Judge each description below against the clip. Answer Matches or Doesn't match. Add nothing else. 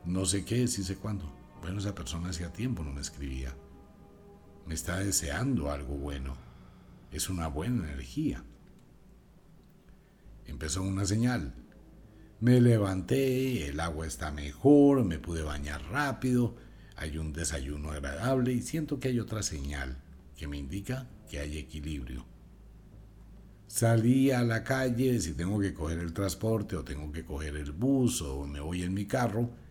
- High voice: Doesn't match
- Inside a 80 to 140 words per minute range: Doesn't match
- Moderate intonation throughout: Doesn't match